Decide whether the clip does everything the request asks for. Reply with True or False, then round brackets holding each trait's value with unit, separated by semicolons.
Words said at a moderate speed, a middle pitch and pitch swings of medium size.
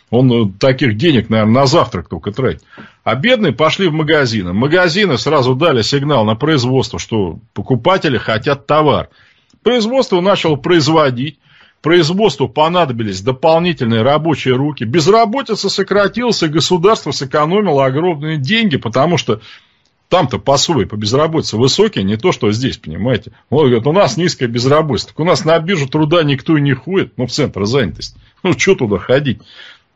False (150 wpm; 150 Hz; 5.8 semitones)